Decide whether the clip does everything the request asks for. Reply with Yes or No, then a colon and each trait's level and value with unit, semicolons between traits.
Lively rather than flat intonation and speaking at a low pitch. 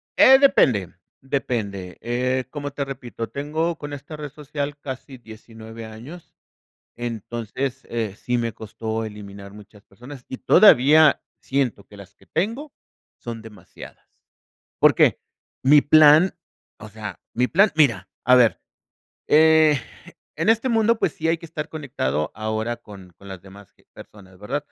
Yes: wide, 5.7 semitones; low, 125 Hz